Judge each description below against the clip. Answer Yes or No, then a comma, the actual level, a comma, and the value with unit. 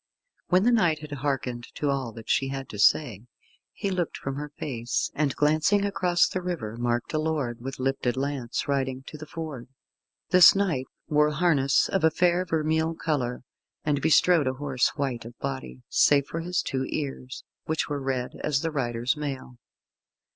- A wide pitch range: No, average, 3.6 semitones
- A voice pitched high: No, medium, 140 Hz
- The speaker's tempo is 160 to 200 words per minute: Yes, average, 175 wpm